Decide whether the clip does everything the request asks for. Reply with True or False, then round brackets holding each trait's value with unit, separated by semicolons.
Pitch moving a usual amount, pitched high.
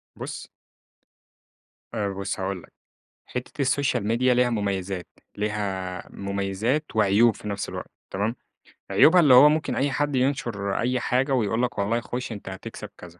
False (4.5 semitones; 110 Hz)